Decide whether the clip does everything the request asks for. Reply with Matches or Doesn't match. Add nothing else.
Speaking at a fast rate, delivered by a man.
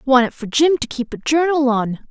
Doesn't match